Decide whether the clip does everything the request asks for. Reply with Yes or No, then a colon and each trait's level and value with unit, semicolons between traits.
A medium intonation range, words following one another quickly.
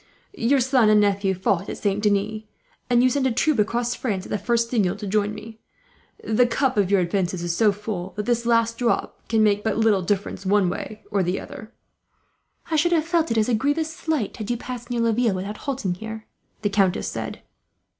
Yes: average, 3.2 semitones; fast, 215 wpm